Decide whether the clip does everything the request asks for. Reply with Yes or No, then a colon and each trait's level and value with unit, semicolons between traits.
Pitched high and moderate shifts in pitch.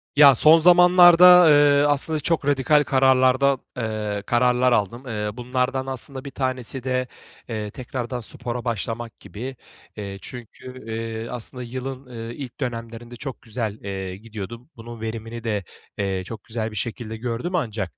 No: low, 120 Hz; average, 3.0 semitones